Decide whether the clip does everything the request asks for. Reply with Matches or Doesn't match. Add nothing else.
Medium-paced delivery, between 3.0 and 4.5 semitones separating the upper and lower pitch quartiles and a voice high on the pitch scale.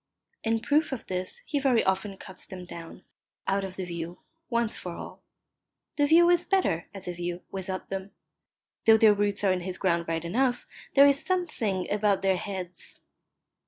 Doesn't match